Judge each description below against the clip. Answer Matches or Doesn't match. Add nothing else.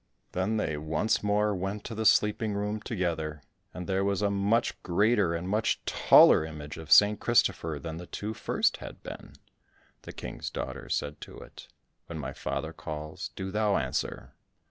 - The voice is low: Matches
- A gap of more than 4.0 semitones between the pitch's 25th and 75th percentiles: Matches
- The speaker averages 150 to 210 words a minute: Matches